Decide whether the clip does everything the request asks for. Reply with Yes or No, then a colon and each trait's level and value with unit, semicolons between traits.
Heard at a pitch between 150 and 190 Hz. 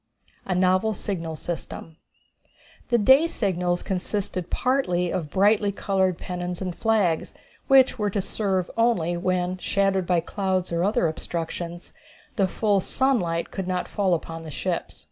Yes: medium, 185 Hz